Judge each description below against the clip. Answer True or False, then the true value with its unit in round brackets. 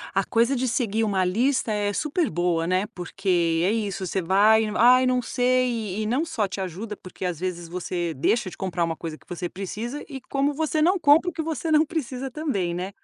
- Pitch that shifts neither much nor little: False (6.2 semitones)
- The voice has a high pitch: True (215 Hz)